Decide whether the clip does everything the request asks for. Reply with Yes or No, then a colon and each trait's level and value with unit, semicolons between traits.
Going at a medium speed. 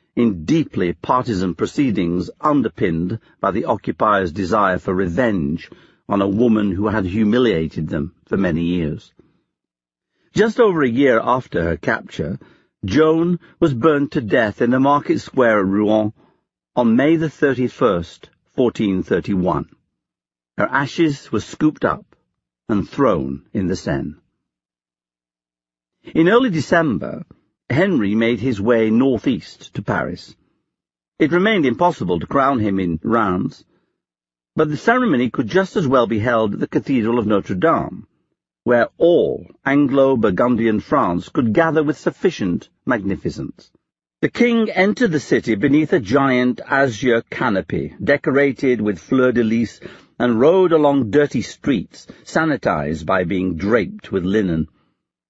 No: slow, 130 wpm